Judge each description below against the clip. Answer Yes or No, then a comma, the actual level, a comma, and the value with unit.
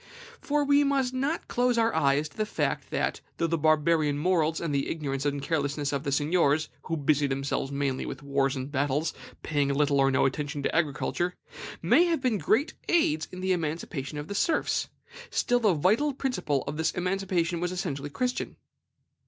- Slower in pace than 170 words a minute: No, average, 185 wpm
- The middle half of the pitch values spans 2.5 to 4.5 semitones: No, average, 5.3 semitones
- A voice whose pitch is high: No, medium, 155 Hz